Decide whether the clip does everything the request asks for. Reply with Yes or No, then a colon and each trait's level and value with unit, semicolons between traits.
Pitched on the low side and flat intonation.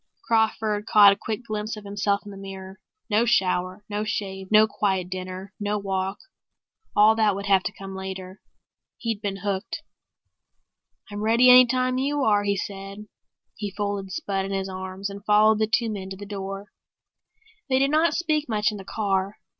No: high, 205 Hz; narrow, 2.0 semitones